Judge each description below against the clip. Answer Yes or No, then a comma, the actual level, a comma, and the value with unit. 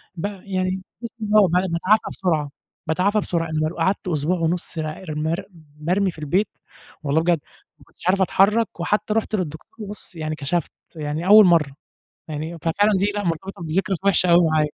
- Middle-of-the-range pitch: Yes, medium, 175 Hz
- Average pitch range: Yes, average, 3.6 semitones